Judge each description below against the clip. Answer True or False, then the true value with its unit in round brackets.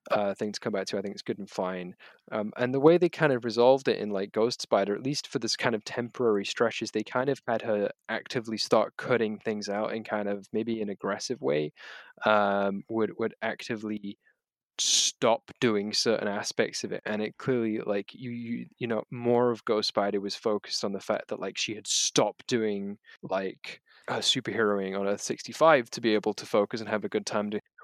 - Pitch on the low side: True (105 Hz)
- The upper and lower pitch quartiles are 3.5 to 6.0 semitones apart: False (2.7 semitones)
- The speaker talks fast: True (220 wpm)